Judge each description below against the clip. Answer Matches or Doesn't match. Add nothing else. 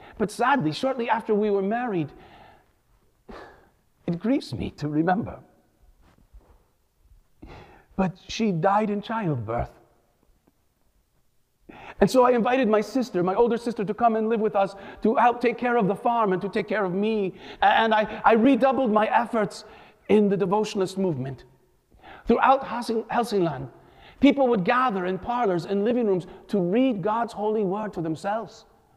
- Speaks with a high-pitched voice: Matches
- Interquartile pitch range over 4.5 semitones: Doesn't match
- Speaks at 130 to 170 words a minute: Matches